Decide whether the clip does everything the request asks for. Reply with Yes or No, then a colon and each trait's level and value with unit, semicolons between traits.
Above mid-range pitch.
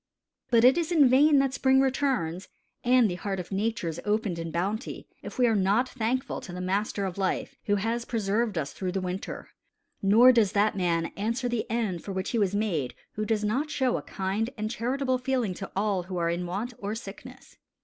Yes: high, 215 Hz